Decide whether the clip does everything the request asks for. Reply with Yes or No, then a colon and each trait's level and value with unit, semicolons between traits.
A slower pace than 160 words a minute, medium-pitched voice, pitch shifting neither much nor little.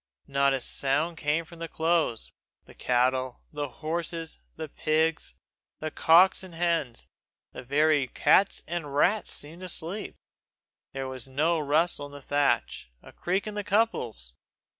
Yes: average, 150 wpm; medium, 155 Hz; average, 3.7 semitones